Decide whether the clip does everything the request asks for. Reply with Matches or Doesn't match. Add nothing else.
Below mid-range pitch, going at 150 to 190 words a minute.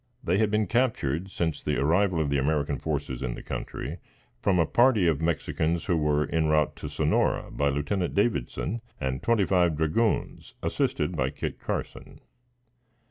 Matches